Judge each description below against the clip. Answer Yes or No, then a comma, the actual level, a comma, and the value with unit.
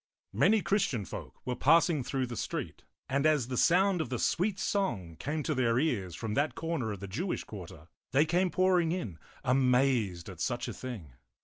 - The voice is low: Yes, low, 130 Hz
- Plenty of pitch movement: Yes, wide, 7.4 semitones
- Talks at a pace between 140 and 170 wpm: No, average, 190 wpm